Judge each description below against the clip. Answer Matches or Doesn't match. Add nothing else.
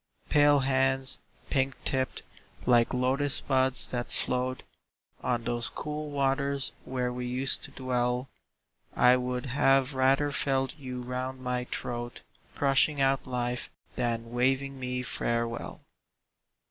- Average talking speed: Doesn't match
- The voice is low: Matches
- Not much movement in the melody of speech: Matches